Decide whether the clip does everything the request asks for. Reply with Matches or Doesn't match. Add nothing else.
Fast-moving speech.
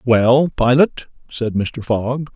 Doesn't match